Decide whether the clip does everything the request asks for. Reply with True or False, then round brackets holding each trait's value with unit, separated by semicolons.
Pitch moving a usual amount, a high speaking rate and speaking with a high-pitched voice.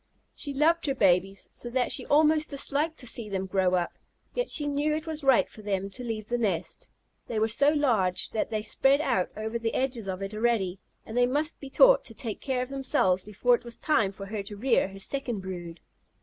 False (5.9 semitones; 225 wpm; 235 Hz)